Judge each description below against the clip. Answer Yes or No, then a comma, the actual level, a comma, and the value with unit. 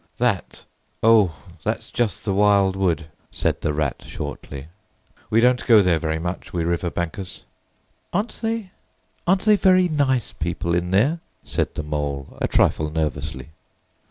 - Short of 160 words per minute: Yes, average, 145 wpm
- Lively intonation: Yes, wide, 7.4 semitones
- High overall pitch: No, very low, 95 Hz